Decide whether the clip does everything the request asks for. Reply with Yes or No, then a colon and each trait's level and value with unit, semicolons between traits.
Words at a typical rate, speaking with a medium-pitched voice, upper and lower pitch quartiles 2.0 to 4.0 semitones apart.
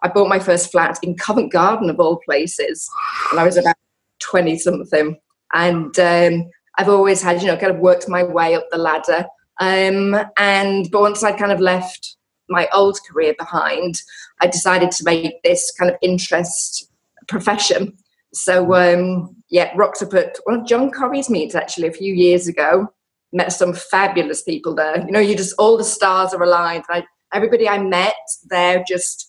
Yes: average, 180 wpm; medium, 180 Hz; average, 2.7 semitones